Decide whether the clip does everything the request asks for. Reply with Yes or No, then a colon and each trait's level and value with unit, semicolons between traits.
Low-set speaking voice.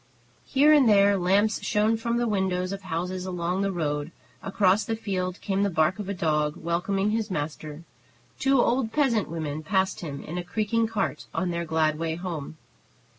No: high, 190 Hz